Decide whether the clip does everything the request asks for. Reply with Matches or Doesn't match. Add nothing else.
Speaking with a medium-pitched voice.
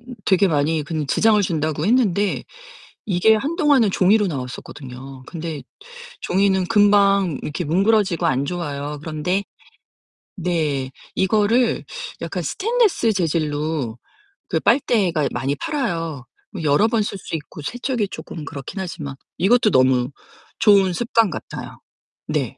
Matches